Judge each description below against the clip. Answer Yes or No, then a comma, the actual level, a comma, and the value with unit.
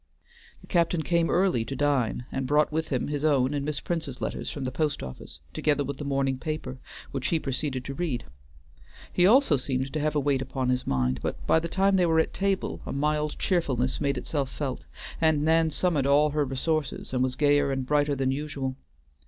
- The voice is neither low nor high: Yes, medium, 145 Hz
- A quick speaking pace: Yes, fast, 210 wpm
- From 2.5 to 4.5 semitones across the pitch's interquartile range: Yes, average, 2.9 semitones